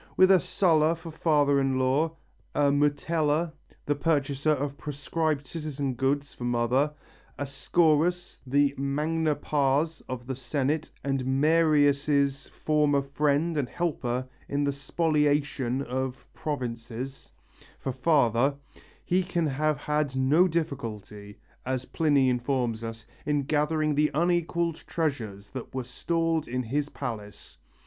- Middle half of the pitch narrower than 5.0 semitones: Yes, average, 2.8 semitones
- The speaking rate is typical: No, slow, 125 wpm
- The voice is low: No, medium, 145 Hz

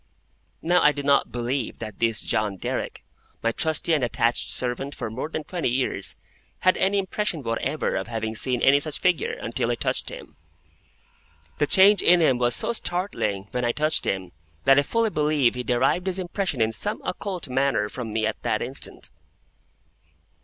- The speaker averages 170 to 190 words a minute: Yes, average, 180 wpm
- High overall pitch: No, low, 135 Hz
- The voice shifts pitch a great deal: Yes, wide, 6.6 semitones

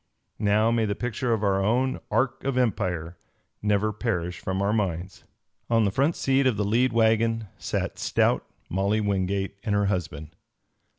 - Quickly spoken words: No, average, 165 wpm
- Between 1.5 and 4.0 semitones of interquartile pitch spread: Yes, average, 3.1 semitones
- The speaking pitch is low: Yes, low, 105 Hz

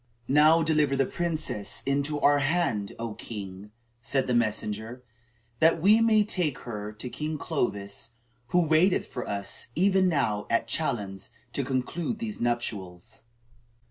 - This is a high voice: No, low, 135 Hz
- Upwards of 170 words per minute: No, average, 140 wpm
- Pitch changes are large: Yes, wide, 7.2 semitones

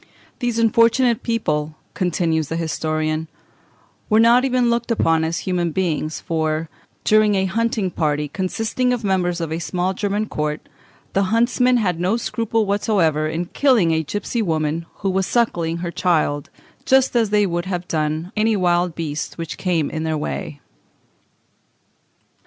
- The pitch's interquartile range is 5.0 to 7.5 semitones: Yes, wide, 5.5 semitones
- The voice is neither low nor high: Yes, medium, 180 Hz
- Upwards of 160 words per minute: No, average, 150 wpm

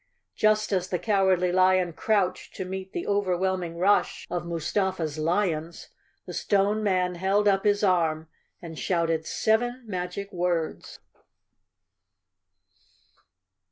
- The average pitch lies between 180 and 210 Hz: Yes, medium, 185 Hz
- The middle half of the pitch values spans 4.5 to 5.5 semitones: No, average, 2.7 semitones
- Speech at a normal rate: No, slow, 115 wpm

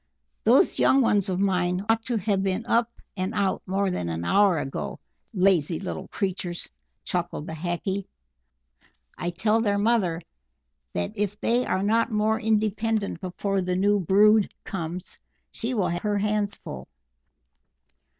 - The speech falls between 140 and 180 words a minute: Yes, average, 150 wpm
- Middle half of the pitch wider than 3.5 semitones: No, average, 2.9 semitones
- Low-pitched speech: No, high, 195 Hz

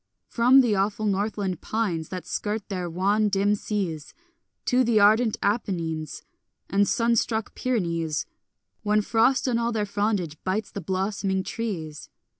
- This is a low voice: No, high, 205 Hz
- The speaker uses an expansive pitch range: No, average, 3.0 semitones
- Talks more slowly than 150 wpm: Yes, average, 140 wpm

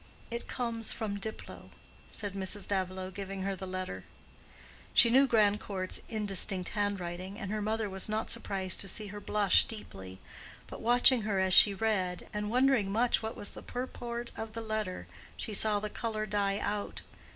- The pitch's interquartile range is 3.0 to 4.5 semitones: No, narrow, 2.5 semitones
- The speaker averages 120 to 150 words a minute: No, average, 170 wpm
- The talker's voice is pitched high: Yes, high, 205 Hz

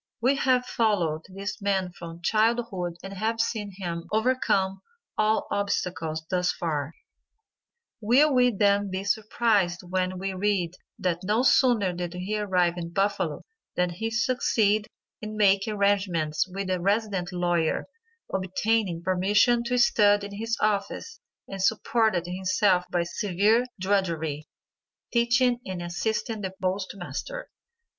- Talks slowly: Yes, slow, 130 wpm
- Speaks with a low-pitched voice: No, high, 195 Hz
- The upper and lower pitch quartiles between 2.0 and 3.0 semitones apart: No, average, 3.5 semitones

